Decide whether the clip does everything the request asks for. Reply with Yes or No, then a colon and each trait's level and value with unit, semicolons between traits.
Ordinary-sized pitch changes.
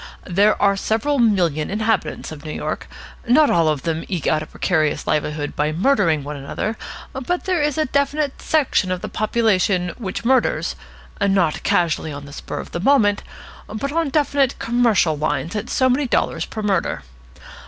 No: wide, 8.2 semitones